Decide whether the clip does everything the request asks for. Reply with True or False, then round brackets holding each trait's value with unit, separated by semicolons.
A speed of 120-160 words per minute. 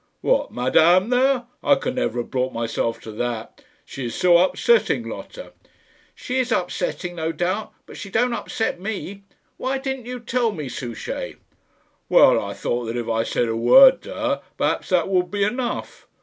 False (180 wpm)